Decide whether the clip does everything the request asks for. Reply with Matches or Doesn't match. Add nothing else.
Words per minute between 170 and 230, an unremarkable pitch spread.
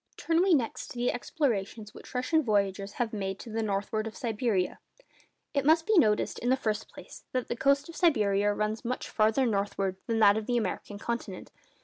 Matches